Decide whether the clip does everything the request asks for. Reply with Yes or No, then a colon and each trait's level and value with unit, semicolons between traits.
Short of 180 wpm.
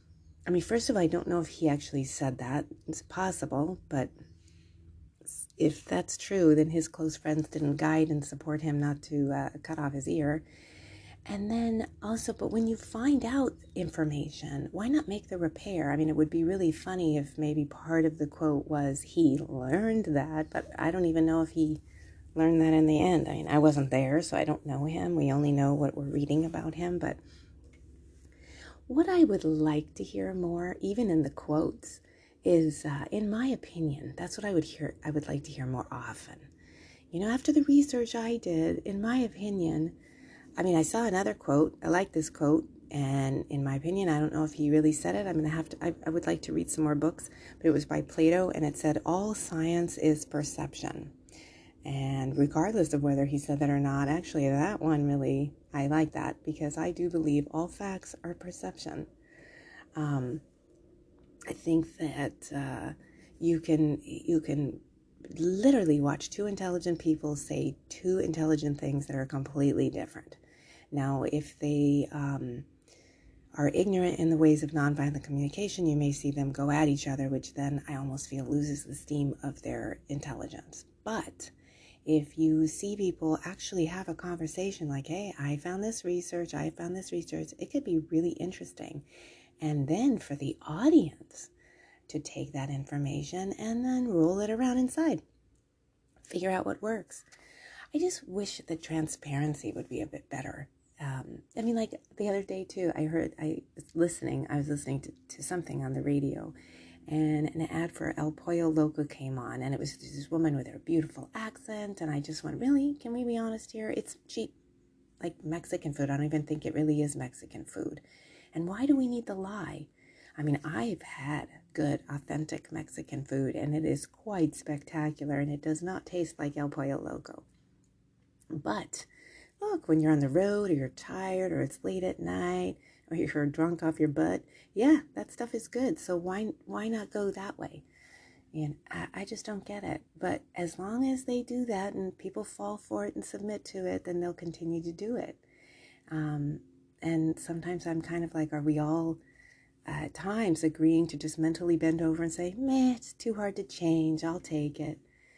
No: average, 190 wpm